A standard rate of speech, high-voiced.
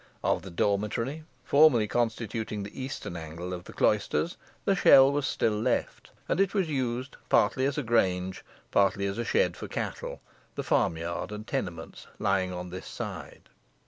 No: average, 170 wpm; low, 105 Hz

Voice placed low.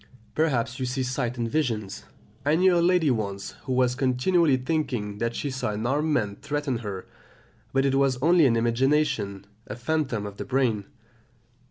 Yes: low, 130 Hz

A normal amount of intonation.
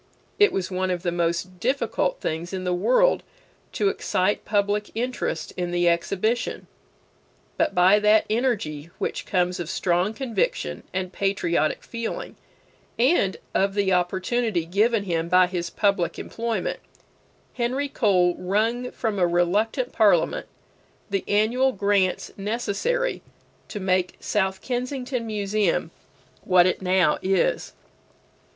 Yes: average, 4.3 semitones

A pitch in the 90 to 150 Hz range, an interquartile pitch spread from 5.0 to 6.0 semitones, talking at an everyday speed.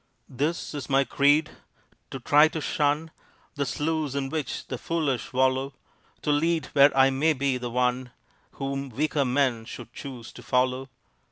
No: medium, 140 Hz; narrow, 2.6 semitones; average, 160 wpm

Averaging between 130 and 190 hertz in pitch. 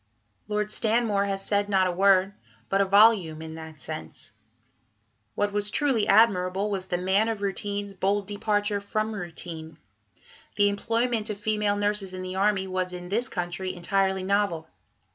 No: high, 200 Hz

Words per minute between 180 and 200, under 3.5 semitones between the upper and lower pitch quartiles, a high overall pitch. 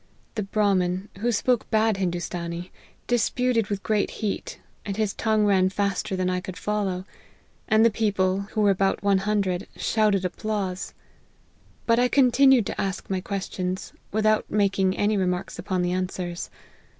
No: average, 150 wpm; average, 2.7 semitones; high, 200 Hz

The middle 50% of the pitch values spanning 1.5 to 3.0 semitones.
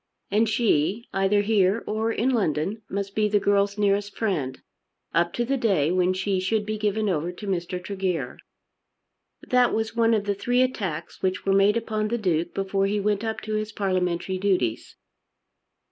Yes: average, 2.7 semitones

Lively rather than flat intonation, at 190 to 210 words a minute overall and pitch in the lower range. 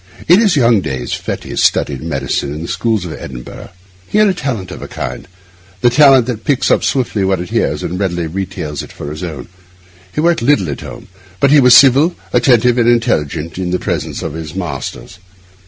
Yes: wide, 7.6 semitones; average, 200 wpm; very low, 95 Hz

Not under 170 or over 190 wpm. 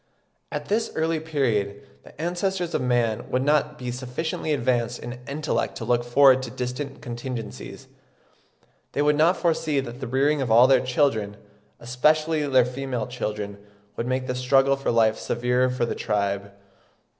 No: average, 160 wpm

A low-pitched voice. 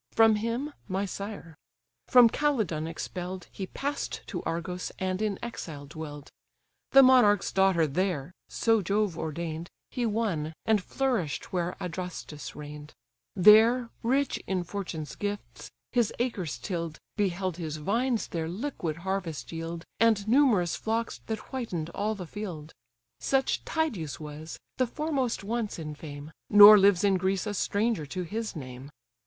No: high, 190 Hz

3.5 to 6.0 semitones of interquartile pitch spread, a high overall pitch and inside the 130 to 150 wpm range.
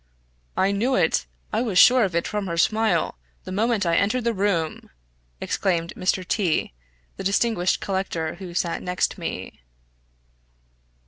Yes: average, 3.8 semitones; high, 195 Hz; average, 145 wpm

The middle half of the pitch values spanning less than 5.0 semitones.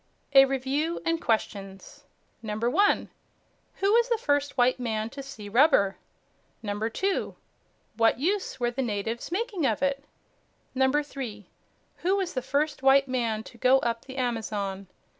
Yes: average, 4.5 semitones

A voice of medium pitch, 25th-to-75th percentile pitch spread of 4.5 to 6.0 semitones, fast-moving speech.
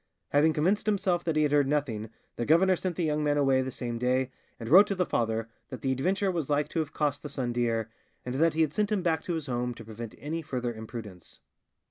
Yes: medium, 145 Hz; average, 5.1 semitones; fast, 245 wpm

